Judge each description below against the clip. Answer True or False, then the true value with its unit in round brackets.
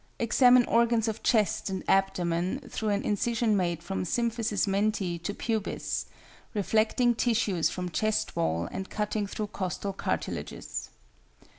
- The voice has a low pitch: False (210 Hz)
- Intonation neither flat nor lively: True (3.3 semitones)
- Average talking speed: False (130 wpm)